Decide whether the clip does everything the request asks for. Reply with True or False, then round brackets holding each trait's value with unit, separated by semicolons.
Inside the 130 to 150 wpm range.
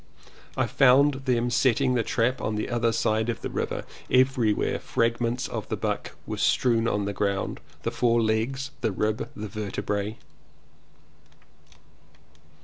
True (140 wpm)